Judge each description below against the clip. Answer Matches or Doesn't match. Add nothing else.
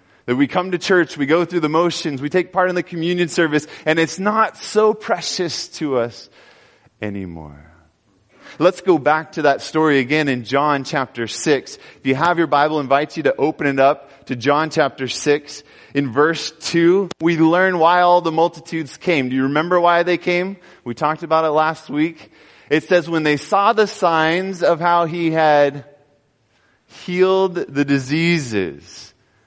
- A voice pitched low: Doesn't match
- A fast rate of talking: Doesn't match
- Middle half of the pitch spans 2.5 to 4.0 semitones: Matches